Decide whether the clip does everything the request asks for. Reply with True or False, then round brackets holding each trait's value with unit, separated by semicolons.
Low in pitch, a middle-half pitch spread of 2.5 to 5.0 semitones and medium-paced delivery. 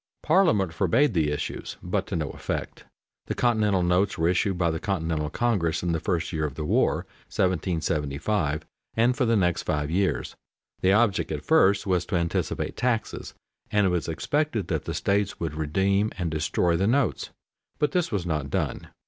True (90 Hz; 4.5 semitones; 180 wpm)